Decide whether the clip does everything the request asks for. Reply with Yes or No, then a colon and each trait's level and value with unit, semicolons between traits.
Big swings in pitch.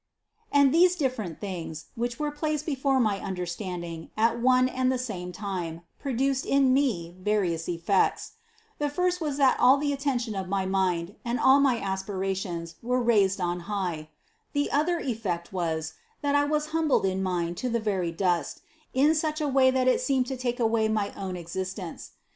Yes: wide, 6.8 semitones